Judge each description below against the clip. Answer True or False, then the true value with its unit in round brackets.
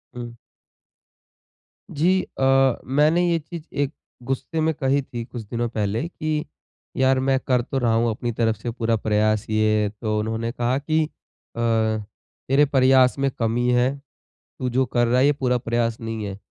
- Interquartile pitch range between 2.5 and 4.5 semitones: True (3.1 semitones)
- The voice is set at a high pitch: False (125 Hz)